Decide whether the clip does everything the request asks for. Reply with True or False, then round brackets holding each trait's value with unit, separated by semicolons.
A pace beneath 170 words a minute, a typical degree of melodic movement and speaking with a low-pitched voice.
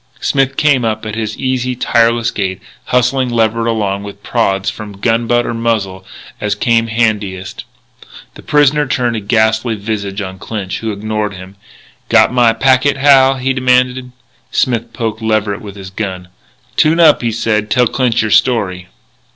True (160 wpm; 3.5 semitones; 115 Hz)